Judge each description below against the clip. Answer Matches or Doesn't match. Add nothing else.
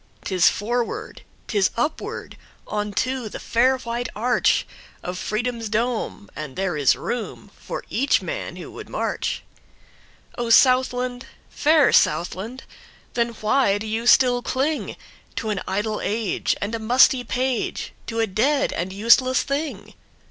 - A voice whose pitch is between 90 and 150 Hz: Doesn't match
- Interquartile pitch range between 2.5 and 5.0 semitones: Matches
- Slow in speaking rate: Matches